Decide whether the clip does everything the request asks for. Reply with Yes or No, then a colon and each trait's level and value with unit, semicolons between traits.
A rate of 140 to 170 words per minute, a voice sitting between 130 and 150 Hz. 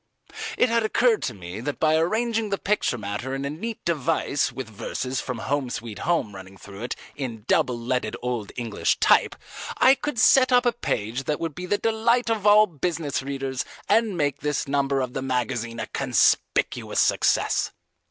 No: average, 180 wpm; medium, 140 Hz